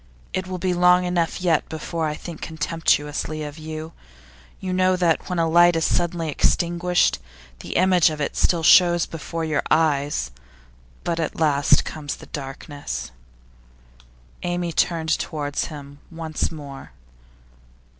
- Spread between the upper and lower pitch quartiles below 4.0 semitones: Yes, narrow, 2.6 semitones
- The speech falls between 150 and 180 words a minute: No, average, 140 wpm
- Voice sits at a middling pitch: Yes, medium, 160 Hz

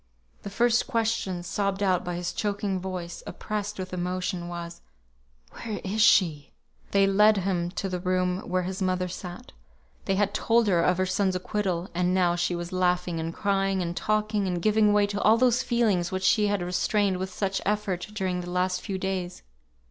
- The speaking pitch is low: No, medium, 185 Hz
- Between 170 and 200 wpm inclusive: Yes, average, 185 wpm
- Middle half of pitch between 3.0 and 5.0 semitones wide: No, narrow, 2.4 semitones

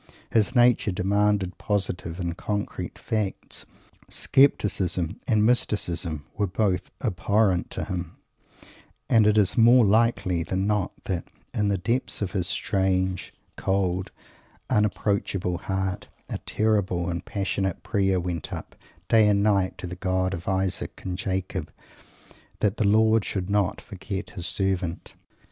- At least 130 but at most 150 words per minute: Yes, slow, 135 wpm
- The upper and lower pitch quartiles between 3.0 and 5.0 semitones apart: No, narrow, 2.4 semitones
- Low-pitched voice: Yes, very low, 95 Hz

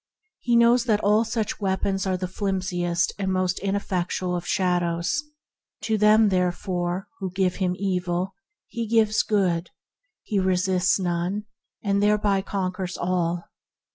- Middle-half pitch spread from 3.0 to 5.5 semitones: No, narrow, 2.5 semitones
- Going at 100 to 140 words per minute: Yes, slow, 135 wpm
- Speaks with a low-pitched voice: No, high, 190 Hz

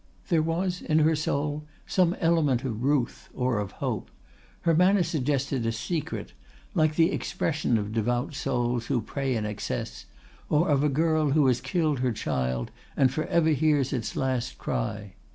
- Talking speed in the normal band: Yes, average, 170 wpm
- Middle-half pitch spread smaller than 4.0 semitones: No, average, 4.7 semitones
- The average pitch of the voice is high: No, medium, 140 Hz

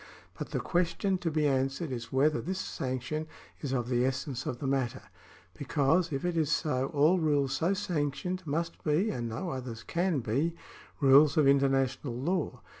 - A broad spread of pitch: No, average, 4.0 semitones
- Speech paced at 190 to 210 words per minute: No, average, 175 wpm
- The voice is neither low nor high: Yes, medium, 145 Hz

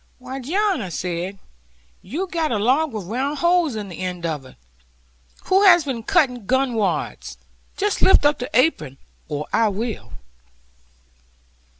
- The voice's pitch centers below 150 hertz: No, very high, 250 Hz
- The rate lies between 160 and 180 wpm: No, average, 150 wpm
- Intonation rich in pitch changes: Yes, wide, 8.2 semitones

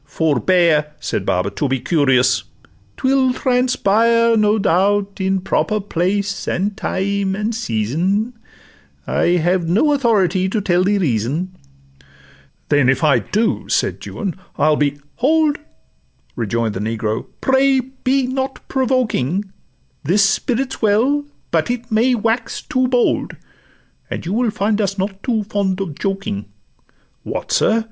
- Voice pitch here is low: No, high, 200 Hz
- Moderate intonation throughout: No, wide, 6.1 semitones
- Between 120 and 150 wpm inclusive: Yes, slow, 135 wpm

